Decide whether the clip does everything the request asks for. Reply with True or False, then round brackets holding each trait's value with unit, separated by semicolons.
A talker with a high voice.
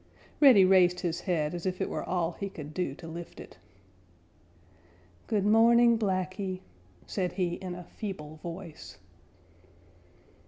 False (180 Hz)